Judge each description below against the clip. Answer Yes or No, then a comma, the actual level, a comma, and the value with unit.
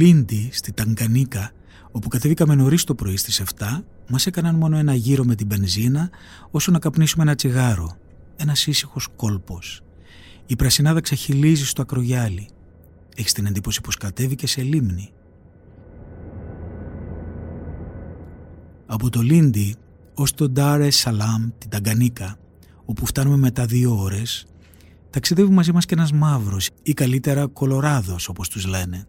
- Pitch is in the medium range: No, low, 110 Hz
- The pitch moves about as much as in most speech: No, wide, 7.5 semitones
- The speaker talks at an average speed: Yes, average, 130 wpm